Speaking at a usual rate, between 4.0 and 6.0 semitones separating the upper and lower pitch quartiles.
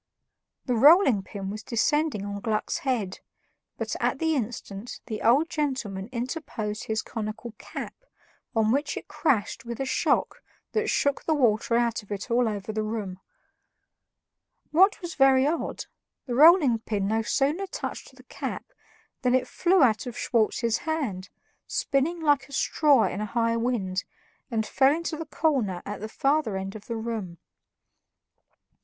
Yes: average, 160 wpm; average, 5.1 semitones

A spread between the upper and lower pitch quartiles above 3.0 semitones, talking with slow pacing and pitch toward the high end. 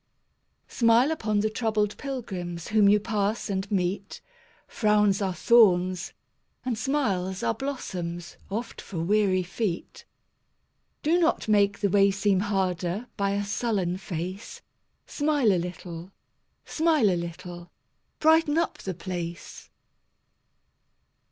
Yes: average, 3.7 semitones; slow, 120 wpm; high, 200 Hz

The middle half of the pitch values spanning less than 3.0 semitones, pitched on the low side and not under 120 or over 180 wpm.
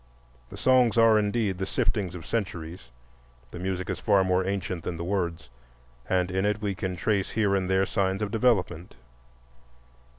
Yes: narrow, 2.4 semitones; very low, 95 Hz; average, 170 wpm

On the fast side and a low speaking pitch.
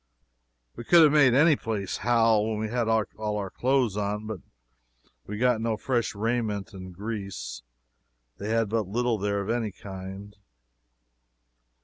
No: average, 145 wpm; low, 110 Hz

